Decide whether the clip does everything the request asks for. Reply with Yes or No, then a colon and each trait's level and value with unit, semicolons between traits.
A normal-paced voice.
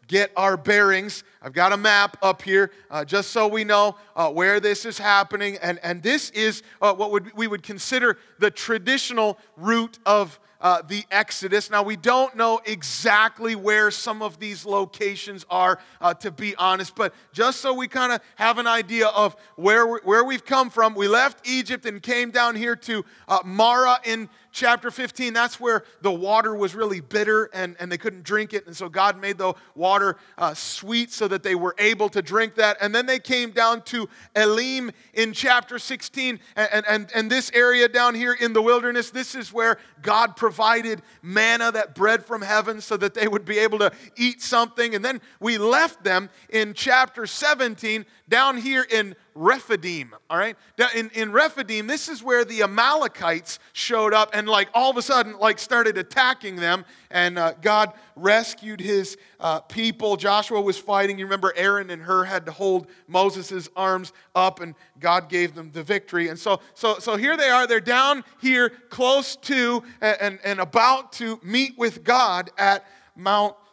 Yes: average, 190 wpm